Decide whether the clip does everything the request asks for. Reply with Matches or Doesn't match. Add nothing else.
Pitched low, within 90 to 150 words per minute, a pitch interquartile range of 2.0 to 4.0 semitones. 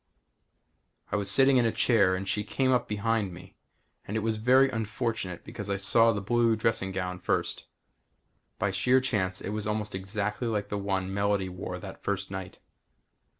Doesn't match